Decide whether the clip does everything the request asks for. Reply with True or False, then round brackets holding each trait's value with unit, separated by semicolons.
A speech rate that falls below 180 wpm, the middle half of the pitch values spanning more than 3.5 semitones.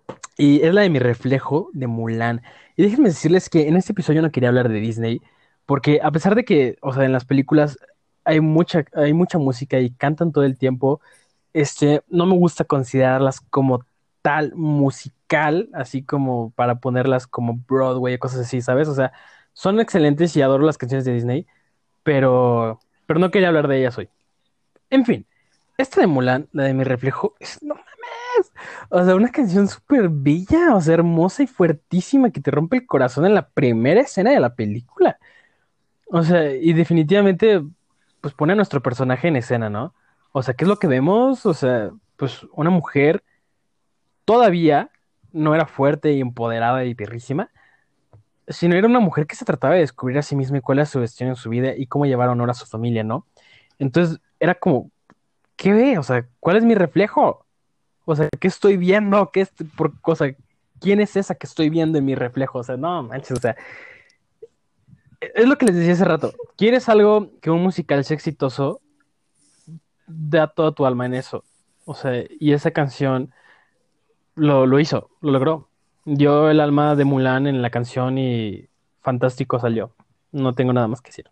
False (185 wpm; 5.2 semitones)